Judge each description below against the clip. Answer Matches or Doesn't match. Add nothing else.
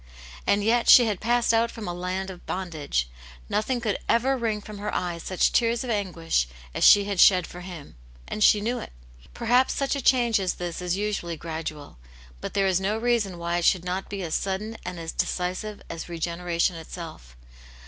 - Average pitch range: Matches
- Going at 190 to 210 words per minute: Matches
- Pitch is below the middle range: Doesn't match